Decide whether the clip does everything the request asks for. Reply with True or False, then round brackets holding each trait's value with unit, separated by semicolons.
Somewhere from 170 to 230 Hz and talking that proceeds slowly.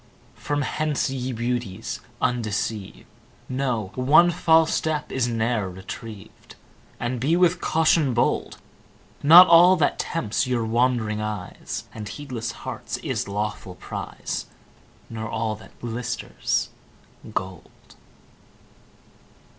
False (120 Hz; 105 wpm)